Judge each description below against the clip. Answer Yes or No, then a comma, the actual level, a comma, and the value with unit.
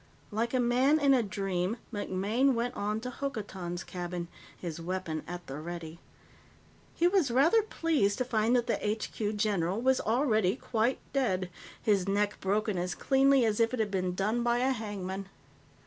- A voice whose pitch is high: Yes, high, 215 Hz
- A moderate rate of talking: Yes, average, 170 wpm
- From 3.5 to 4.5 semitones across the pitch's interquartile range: No, average, 5.0 semitones